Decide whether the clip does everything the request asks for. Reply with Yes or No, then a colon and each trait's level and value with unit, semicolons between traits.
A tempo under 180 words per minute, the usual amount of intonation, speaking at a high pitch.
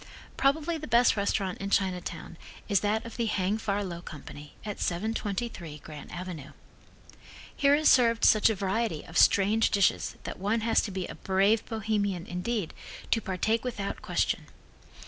Yes: average, 160 wpm; average, 3.6 semitones; high, 205 Hz